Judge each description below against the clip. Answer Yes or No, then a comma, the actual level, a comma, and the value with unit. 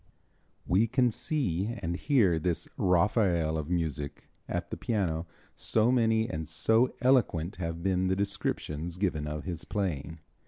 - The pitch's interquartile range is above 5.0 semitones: Yes, wide, 5.4 semitones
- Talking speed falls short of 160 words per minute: Yes, average, 145 wpm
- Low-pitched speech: Yes, very low, 90 Hz